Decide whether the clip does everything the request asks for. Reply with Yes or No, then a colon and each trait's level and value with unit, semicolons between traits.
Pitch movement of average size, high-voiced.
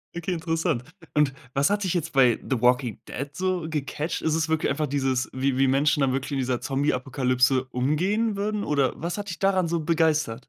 No: average, 4.2 semitones; medium, 150 Hz